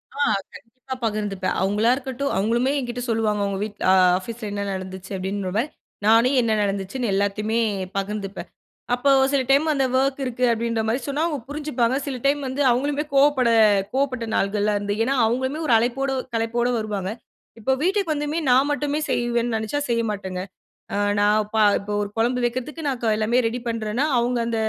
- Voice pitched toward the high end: Yes, high, 235 Hz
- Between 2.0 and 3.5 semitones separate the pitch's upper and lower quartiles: No, average, 4.2 semitones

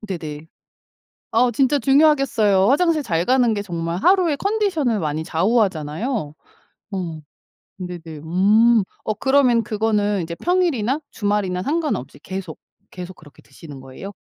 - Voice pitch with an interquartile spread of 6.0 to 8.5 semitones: Yes, wide, 7.4 semitones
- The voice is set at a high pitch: Yes, high, 210 Hz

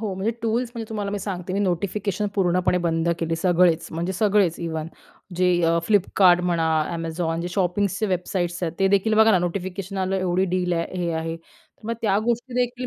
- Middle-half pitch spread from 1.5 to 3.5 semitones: Yes, average, 2.9 semitones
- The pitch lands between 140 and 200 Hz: Yes, medium, 185 Hz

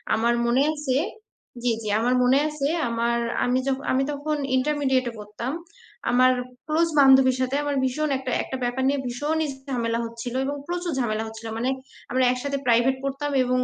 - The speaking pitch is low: No, very high, 260 Hz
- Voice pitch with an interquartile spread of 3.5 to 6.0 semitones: No, average, 2.8 semitones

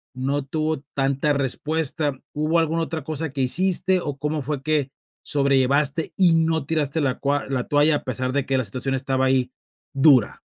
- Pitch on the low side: No, medium, 145 Hz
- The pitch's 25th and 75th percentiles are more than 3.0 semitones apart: No, average, 2.7 semitones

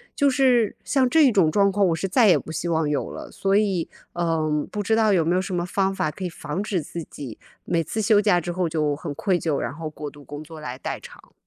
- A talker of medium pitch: Yes, medium, 175 Hz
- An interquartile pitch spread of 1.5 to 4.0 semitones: No, average, 4.7 semitones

